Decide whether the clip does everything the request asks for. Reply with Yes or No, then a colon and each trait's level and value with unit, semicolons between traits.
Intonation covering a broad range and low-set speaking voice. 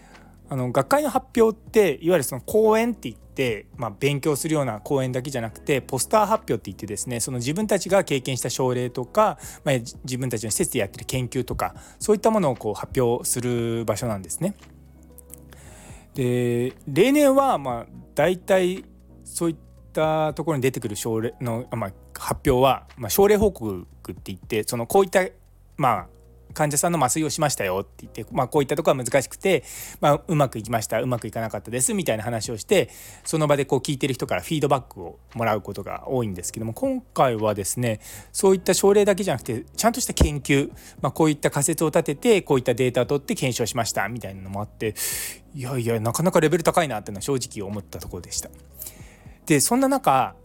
Yes: wide, 6.2 semitones; low, 130 Hz